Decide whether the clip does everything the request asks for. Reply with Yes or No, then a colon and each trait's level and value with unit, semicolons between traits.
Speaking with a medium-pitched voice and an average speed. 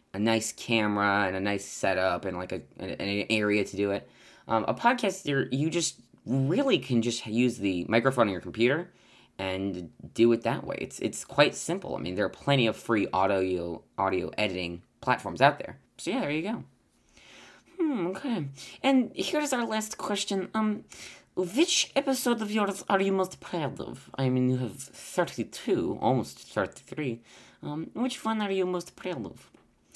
No: low, 125 Hz; average, 175 wpm